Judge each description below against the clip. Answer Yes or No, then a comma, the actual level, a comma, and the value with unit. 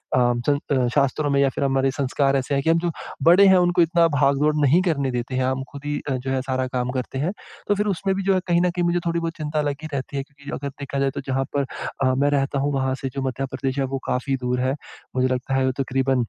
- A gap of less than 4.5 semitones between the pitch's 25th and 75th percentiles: Yes, average, 2.7 semitones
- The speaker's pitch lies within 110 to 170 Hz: Yes, medium, 140 Hz